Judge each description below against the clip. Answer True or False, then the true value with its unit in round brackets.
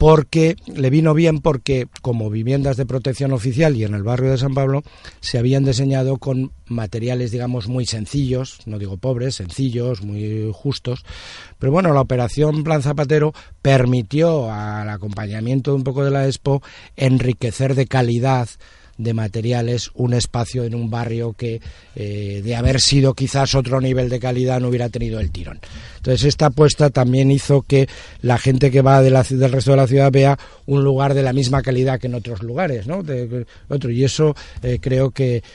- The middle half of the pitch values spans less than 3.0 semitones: True (2.4 semitones)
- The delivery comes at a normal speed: True (180 wpm)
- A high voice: False (130 Hz)